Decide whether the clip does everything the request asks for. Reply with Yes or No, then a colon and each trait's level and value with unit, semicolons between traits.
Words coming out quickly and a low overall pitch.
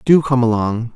No: average, 190 wpm; low, 125 Hz